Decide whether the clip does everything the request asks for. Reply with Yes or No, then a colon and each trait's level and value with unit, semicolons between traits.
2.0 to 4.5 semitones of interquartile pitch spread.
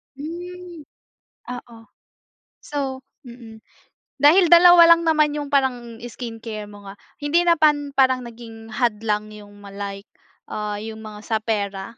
No: wide, 5.4 semitones